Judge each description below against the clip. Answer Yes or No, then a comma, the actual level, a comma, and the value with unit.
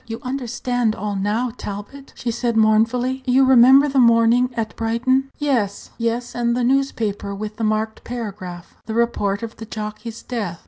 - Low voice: No, high, 230 Hz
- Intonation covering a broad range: No, narrow, 2.6 semitones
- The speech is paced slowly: No, average, 165 wpm